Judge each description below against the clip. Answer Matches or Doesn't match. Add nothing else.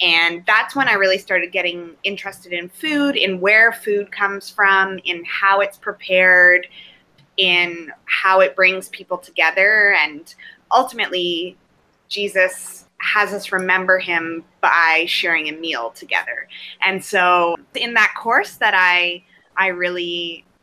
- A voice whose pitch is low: Doesn't match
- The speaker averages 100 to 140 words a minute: Matches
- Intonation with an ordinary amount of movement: Doesn't match